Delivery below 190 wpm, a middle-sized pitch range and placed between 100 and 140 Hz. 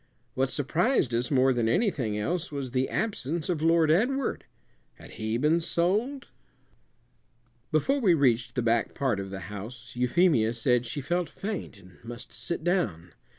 No: average, 155 wpm; wide, 6.7 semitones; low, 135 Hz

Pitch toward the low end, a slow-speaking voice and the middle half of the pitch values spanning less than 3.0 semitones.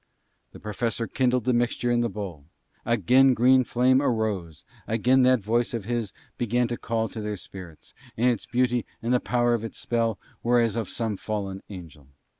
No: low, 115 Hz; average, 185 wpm; narrow, 2.6 semitones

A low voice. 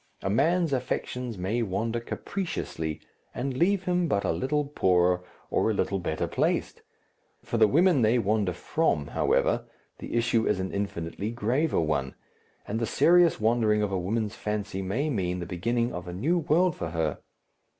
Yes: low, 110 Hz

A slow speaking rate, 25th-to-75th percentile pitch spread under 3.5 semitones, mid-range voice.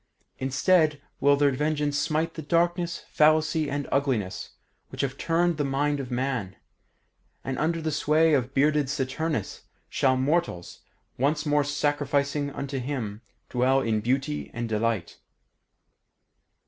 Yes: slow, 130 wpm; average, 2.7 semitones; medium, 145 Hz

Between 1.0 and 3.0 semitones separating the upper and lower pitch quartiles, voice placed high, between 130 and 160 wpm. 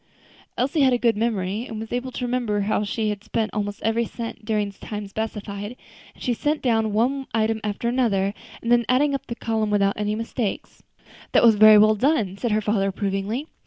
No: narrow, 2.6 semitones; high, 220 Hz; fast, 205 wpm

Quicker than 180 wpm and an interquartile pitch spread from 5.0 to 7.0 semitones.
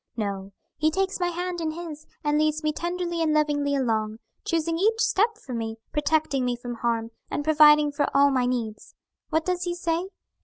Yes: average, 190 wpm; average, 5.3 semitones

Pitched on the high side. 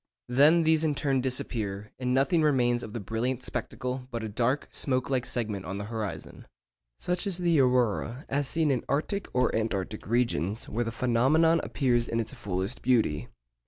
No: low, 125 Hz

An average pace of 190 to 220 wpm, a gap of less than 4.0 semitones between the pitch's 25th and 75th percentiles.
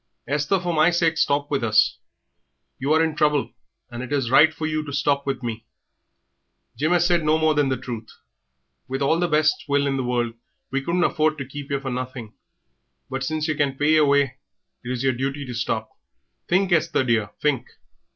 Yes: fast, 205 wpm; average, 3.2 semitones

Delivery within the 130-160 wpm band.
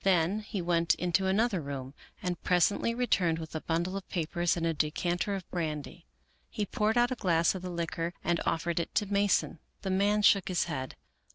No: average, 200 wpm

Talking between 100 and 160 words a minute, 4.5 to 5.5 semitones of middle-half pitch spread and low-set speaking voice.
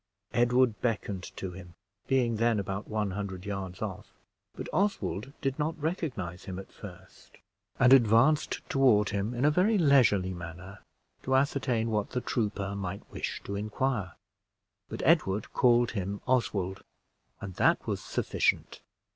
Yes: average, 145 wpm; average, 5.1 semitones; low, 105 Hz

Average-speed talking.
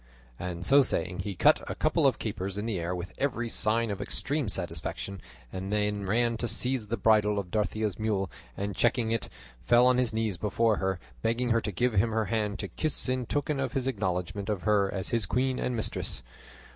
No: fast, 210 wpm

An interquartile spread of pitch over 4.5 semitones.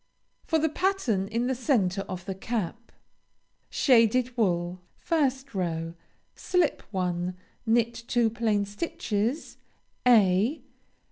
Yes: average, 5.3 semitones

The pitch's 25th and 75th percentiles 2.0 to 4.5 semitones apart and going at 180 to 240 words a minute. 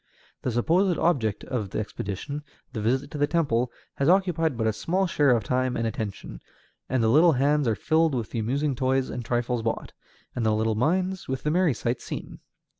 No: wide, 5.6 semitones; average, 200 wpm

